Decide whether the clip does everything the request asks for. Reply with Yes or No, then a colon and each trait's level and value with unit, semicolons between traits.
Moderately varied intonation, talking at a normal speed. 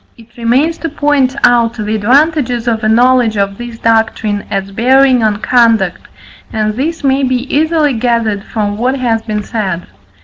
Yes: average, 3.2 semitones; average, 165 wpm